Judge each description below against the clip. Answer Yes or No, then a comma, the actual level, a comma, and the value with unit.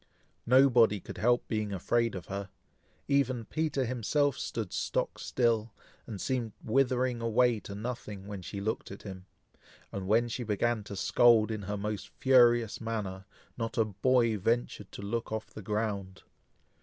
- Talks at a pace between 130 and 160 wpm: Yes, average, 155 wpm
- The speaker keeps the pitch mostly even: No, average, 3.0 semitones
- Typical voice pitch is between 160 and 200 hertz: No, low, 110 Hz